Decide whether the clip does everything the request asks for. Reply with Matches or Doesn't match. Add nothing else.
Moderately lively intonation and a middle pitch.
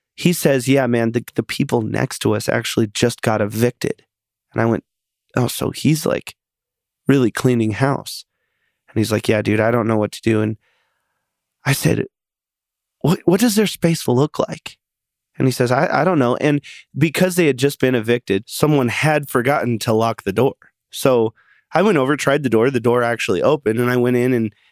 Doesn't match